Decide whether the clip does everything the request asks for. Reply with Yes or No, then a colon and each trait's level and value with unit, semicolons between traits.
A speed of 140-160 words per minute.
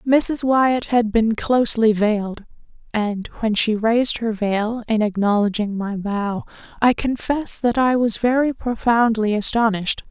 Yes: average, 145 wpm